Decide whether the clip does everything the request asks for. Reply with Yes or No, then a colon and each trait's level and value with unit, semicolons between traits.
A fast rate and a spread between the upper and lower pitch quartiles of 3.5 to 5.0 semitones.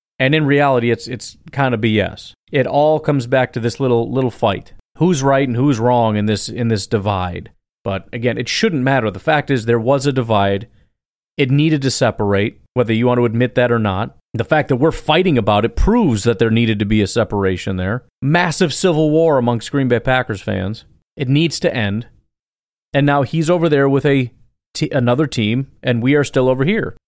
Yes: fast, 210 wpm; average, 4.1 semitones